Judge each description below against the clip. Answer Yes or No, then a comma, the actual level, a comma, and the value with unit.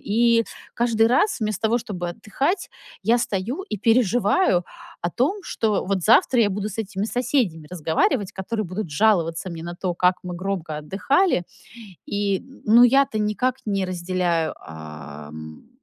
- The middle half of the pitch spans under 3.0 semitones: No, average, 5.0 semitones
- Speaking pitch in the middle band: No, high, 200 Hz